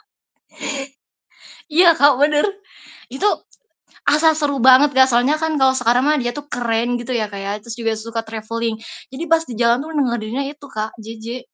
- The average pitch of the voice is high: Yes, very high, 250 Hz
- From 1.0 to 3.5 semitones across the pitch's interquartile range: No, average, 4.1 semitones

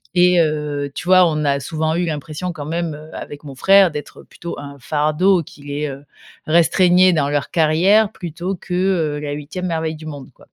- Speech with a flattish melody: No, average, 3.2 semitones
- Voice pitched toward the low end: No, medium, 155 Hz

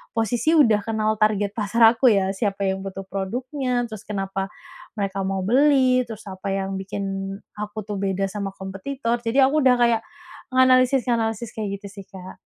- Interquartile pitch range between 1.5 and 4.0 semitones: Yes, average, 3.6 semitones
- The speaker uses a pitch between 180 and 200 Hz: No, high, 215 Hz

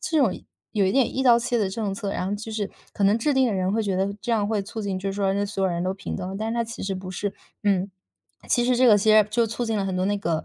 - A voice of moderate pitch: No, high, 205 Hz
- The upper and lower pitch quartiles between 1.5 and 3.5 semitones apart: Yes, average, 2.8 semitones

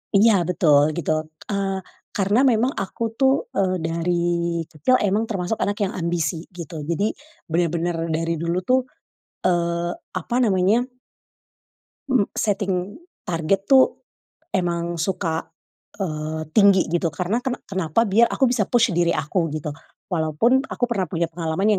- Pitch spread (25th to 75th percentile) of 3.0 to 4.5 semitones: Yes, average, 3.7 semitones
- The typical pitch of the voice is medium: Yes, medium, 180 Hz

